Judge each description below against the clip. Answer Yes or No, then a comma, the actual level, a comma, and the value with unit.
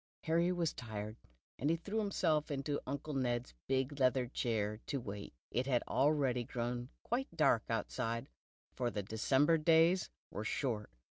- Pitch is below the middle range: Yes, low, 130 Hz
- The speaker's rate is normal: Yes, average, 145 wpm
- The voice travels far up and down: No, average, 4.7 semitones